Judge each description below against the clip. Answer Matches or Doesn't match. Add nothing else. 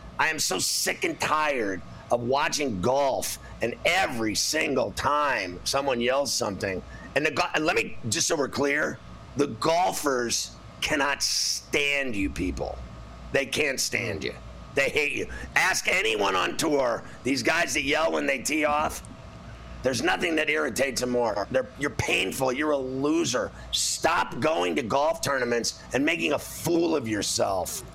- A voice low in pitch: Matches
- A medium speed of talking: Matches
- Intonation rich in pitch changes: Doesn't match